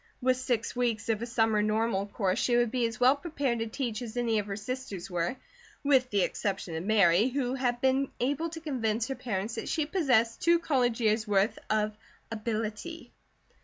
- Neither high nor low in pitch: No, high, 230 Hz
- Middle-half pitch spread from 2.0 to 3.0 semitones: No, average, 3.4 semitones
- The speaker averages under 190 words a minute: No, average, 195 wpm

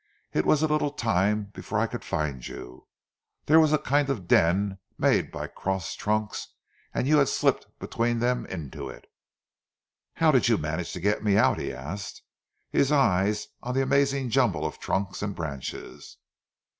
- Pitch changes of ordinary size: No, wide, 7.0 semitones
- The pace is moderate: Yes, average, 170 wpm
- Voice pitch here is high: No, low, 105 Hz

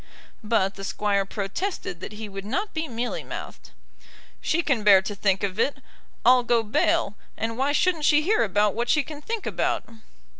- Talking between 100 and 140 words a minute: No, average, 185 wpm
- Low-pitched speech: No, high, 225 Hz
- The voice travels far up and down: Yes, wide, 6.7 semitones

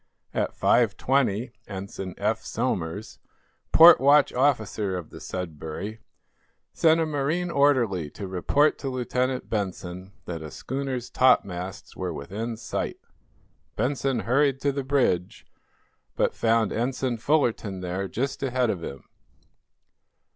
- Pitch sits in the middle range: No, low, 115 Hz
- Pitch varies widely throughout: Yes, wide, 6.3 semitones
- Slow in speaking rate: Yes, slow, 120 wpm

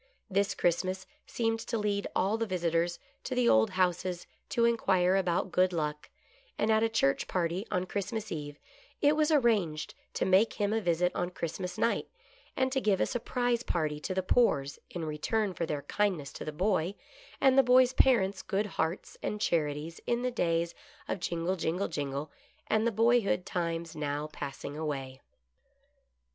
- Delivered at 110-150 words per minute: No, average, 175 wpm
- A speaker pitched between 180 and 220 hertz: Yes, medium, 185 Hz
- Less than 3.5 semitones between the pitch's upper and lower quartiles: No, average, 5.1 semitones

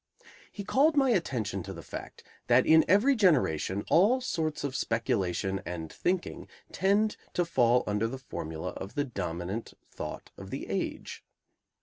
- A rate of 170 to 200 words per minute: No, average, 150 wpm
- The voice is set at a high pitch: No, low, 130 Hz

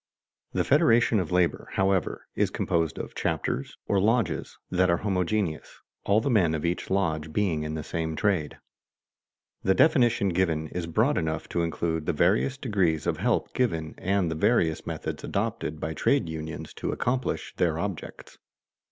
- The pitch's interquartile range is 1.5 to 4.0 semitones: No, average, 4.4 semitones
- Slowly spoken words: No, average, 160 wpm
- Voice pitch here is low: Yes, very low, 90 Hz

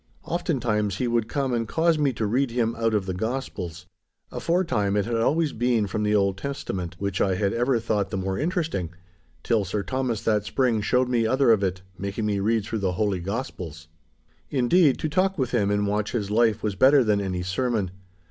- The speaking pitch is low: Yes, low, 110 Hz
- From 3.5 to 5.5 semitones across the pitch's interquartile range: Yes, average, 4.4 semitones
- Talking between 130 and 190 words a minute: No, fast, 205 wpm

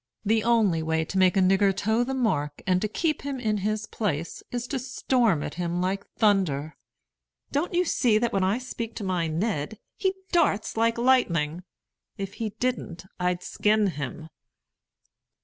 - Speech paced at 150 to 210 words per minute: Yes, average, 170 wpm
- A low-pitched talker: No, high, 205 Hz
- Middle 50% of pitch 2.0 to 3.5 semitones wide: No, average, 5.0 semitones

